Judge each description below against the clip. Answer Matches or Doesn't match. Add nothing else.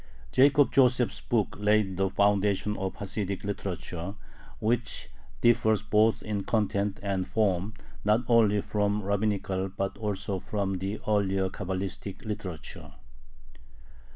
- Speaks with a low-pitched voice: Matches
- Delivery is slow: Matches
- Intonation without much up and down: Matches